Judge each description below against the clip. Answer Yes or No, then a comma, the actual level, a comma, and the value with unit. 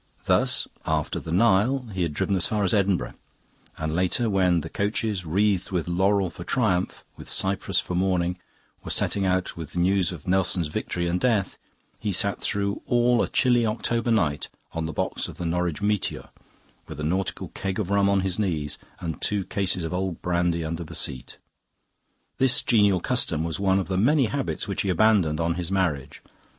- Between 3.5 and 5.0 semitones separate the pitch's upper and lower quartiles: No, average, 2.9 semitones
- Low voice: Yes, very low, 95 Hz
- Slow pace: No, average, 190 wpm